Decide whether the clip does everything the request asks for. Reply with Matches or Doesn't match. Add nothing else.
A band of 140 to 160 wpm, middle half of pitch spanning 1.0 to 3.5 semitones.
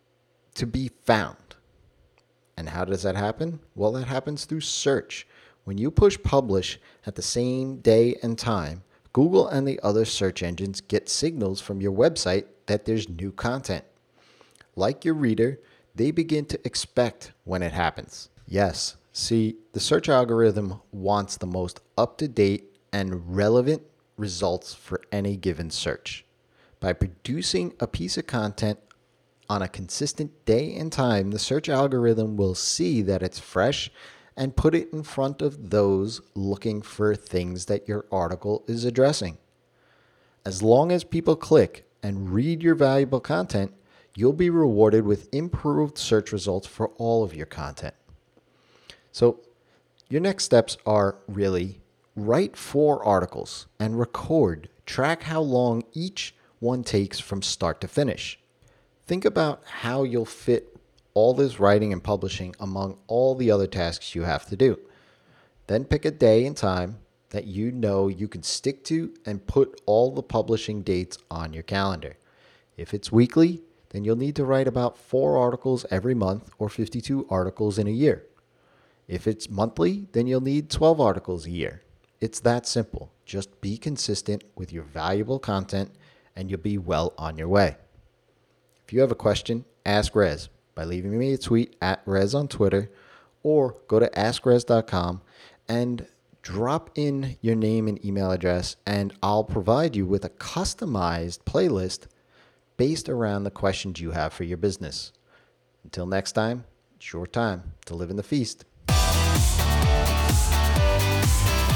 Doesn't match